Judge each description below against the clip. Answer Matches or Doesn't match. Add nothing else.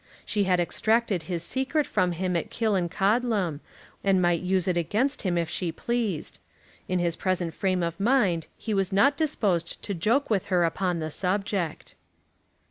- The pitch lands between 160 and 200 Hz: Matches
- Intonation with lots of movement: Doesn't match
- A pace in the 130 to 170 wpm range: Matches